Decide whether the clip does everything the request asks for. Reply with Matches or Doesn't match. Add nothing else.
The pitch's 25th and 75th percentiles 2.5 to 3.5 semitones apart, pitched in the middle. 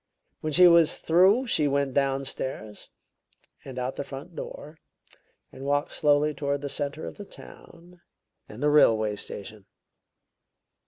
Matches